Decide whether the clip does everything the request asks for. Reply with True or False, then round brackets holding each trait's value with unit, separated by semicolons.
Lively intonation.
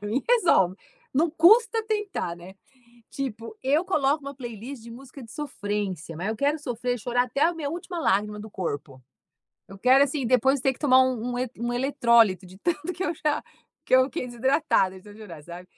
True (5.7 semitones)